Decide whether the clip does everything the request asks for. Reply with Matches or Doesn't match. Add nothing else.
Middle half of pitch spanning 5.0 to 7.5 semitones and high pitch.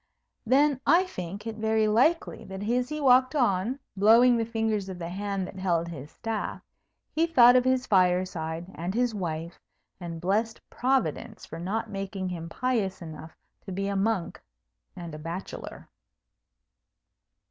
Matches